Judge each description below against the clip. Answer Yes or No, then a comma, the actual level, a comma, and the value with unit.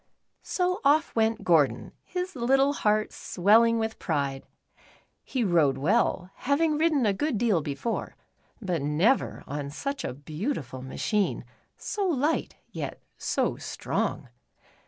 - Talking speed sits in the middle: No, slow, 125 wpm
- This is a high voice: Yes, high, 220 Hz